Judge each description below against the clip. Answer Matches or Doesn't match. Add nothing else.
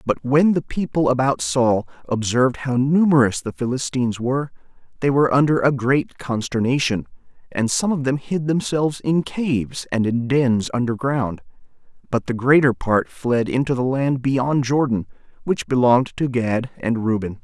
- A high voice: Doesn't match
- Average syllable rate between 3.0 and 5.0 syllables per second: Matches